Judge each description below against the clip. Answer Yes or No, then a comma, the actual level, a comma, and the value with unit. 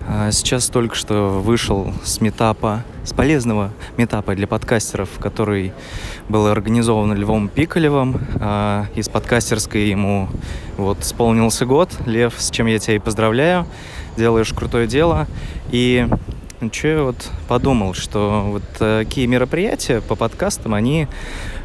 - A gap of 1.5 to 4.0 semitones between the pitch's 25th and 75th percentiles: Yes, average, 2.8 semitones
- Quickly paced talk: No, average, 120 wpm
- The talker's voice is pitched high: No, low, 110 Hz